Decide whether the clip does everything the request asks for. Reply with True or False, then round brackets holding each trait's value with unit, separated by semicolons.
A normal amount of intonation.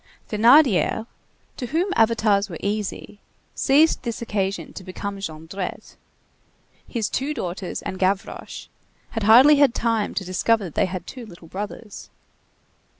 True (3.6 semitones)